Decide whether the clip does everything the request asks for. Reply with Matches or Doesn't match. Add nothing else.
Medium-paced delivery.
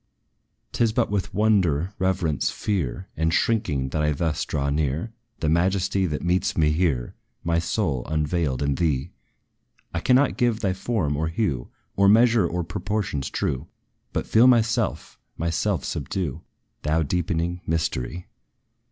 Matches